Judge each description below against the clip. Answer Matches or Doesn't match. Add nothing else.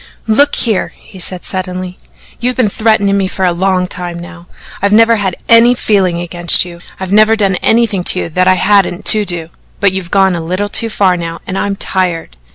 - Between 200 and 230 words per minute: Matches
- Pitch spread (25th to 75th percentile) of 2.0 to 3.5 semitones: Matches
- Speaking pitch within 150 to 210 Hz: Matches